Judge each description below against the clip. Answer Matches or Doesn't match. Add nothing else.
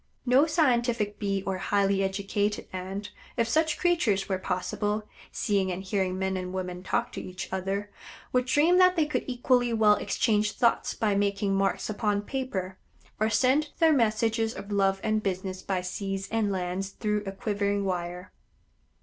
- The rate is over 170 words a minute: Doesn't match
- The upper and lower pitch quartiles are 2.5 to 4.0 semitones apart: Matches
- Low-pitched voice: Doesn't match